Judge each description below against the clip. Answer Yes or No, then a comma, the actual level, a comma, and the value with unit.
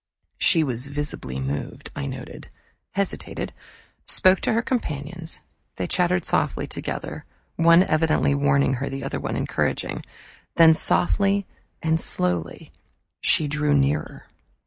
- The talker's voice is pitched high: No, medium, 150 Hz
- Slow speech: Yes, slow, 120 wpm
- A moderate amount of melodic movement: Yes, average, 3.9 semitones